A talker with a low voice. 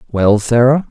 Yes: low, 120 Hz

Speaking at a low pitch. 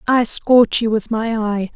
No: high, 225 Hz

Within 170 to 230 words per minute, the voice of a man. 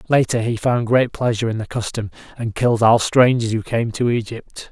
Yes: fast, 205 wpm; male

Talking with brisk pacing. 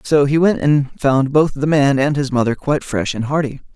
Yes: fast, 240 wpm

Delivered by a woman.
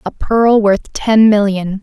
Yes: female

